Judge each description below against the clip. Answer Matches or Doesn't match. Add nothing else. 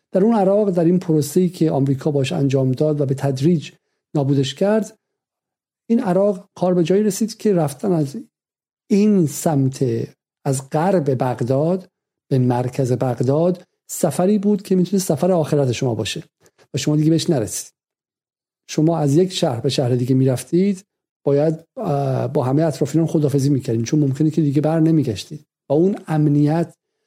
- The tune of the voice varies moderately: Matches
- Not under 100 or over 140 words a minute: Doesn't match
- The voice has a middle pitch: Matches